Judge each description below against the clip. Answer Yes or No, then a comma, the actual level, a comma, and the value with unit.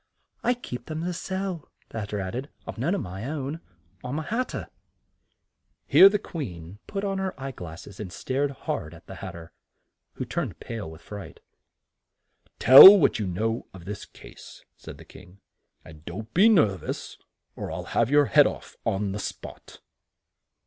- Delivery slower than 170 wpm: No, average, 185 wpm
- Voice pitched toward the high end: No, low, 125 Hz